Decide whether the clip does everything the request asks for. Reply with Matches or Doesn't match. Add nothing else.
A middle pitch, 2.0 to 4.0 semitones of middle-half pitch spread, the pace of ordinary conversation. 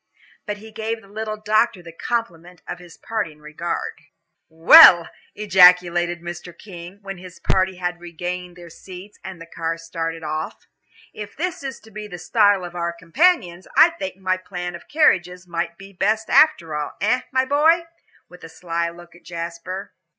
Matches